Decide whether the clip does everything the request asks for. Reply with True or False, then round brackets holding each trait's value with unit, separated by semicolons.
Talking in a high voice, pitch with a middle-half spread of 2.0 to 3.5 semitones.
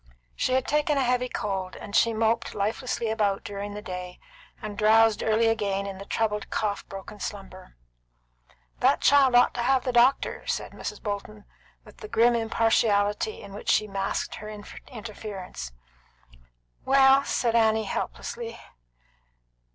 True (220 Hz; 2.9 semitones)